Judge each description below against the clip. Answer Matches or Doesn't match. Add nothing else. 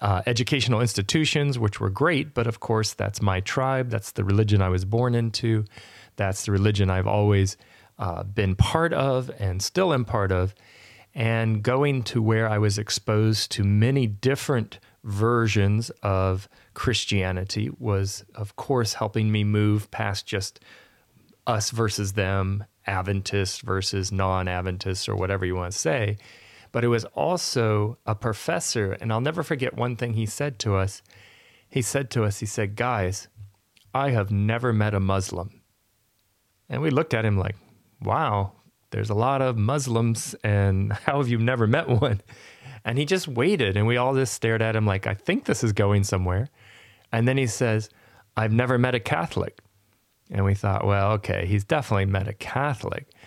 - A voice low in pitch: Matches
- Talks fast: Doesn't match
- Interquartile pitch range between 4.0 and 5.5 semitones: Doesn't match